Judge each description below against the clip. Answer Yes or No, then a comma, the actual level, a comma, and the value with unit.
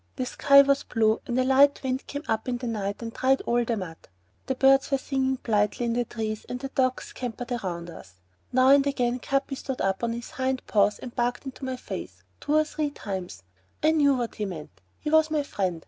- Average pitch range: Yes, average, 3.8 semitones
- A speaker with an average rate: No, fast, 230 wpm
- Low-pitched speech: No, very high, 250 Hz